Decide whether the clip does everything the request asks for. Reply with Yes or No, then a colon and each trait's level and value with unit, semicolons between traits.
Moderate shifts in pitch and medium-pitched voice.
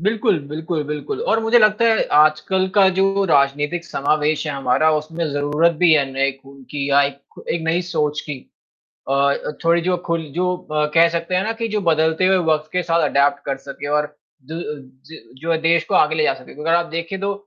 Yes: average, 3.5 semitones; medium, 160 Hz